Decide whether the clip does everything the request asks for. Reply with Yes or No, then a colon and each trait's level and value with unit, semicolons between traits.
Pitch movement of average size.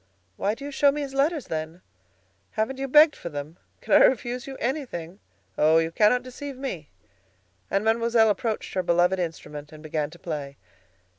No: wide, 8.4 semitones